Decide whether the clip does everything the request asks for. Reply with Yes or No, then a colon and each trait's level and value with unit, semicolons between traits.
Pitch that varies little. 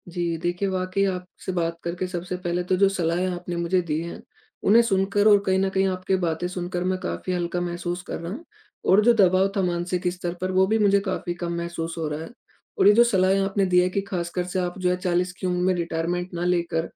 Yes: narrow, 1.5 semitones